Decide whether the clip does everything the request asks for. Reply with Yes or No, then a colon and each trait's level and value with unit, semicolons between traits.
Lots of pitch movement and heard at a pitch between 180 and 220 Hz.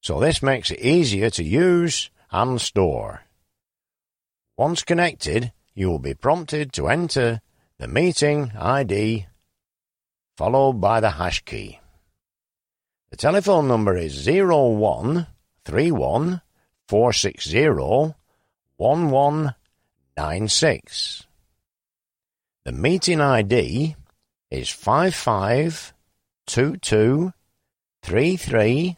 No: wide, 7.4 semitones; low, 130 Hz